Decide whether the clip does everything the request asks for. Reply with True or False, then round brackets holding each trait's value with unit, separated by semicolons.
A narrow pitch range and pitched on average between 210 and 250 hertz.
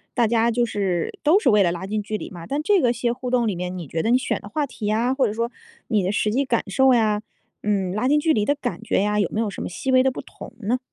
False (3.7 semitones; 225 Hz)